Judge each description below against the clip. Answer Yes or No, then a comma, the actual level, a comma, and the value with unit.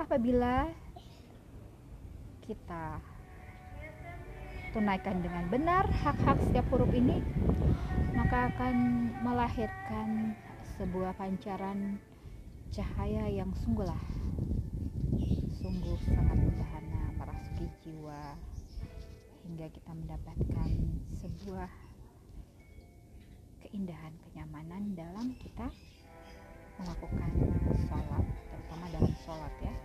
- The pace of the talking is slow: Yes, slow, 70 wpm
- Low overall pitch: Yes, low, 110 Hz